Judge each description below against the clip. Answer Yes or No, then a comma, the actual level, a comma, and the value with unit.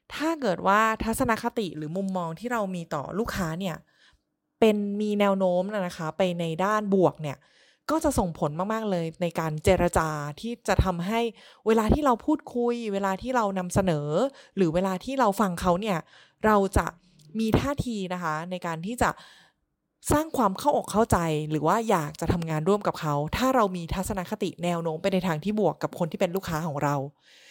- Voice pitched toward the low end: No, high, 190 Hz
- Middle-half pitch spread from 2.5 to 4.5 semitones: No, average, 4.9 semitones